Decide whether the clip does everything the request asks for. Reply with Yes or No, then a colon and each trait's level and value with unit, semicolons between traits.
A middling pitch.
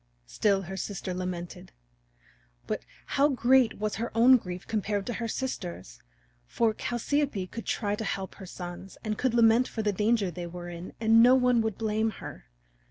No: high, 215 Hz